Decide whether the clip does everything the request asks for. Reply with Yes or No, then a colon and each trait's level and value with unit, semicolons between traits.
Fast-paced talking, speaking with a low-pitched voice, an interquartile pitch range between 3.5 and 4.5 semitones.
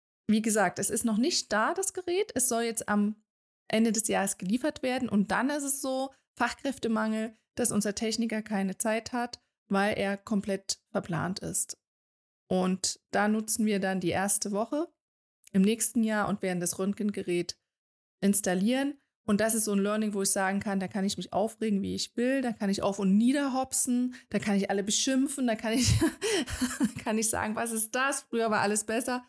No: fast, 195 wpm; high, 220 Hz; average, 3.8 semitones